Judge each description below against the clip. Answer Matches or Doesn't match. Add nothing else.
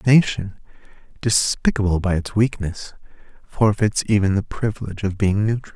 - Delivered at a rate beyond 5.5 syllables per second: Doesn't match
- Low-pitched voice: Matches